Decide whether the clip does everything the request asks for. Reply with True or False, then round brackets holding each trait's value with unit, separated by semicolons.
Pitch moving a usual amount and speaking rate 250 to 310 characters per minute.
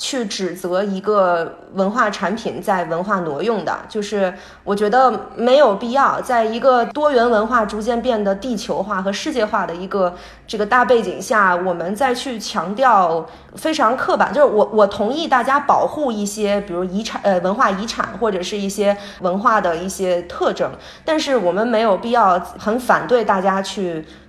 True (4.4 semitones; 265 characters per minute)